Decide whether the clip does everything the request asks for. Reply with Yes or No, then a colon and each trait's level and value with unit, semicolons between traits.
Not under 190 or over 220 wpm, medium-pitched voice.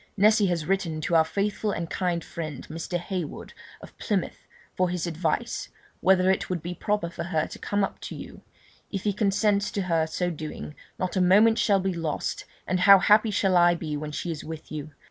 Yes: fast, 205 wpm; medium, 180 Hz